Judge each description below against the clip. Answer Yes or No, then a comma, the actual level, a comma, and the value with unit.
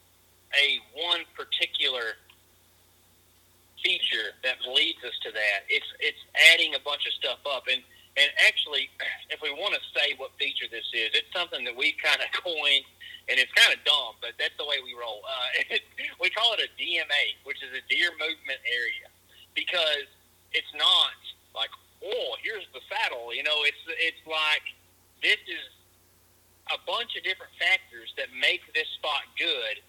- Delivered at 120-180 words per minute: Yes, average, 170 wpm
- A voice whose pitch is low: No, medium, 165 Hz